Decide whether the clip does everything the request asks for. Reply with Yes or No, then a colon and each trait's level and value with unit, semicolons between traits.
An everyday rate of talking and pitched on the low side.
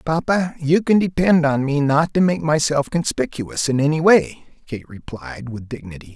No: average, 175 wpm; medium, 150 Hz